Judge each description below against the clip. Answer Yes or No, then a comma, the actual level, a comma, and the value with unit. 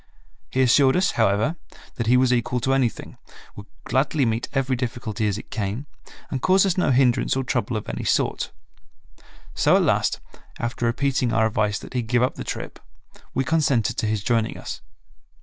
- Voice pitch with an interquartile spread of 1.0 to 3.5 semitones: Yes, average, 3.2 semitones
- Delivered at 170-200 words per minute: Yes, average, 185 wpm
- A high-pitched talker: No, low, 125 Hz